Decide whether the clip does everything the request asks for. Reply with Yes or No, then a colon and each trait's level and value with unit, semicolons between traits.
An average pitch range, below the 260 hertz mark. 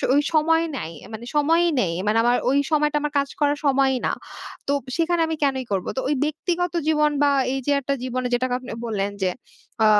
No: average, 3.4 semitones; very high, 280 Hz